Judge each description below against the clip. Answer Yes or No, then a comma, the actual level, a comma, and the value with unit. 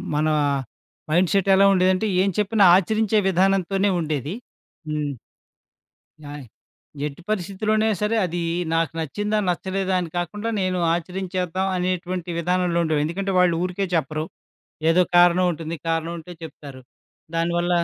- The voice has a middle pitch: Yes, medium, 180 Hz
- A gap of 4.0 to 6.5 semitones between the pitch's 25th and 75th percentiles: No, average, 2.8 semitones